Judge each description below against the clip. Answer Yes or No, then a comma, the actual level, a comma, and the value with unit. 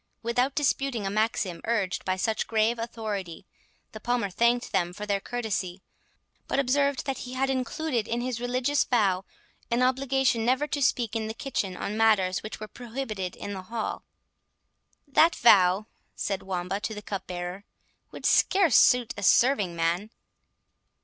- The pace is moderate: Yes, average, 155 wpm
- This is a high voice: Yes, high, 225 Hz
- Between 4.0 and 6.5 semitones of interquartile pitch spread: Yes, average, 4.4 semitones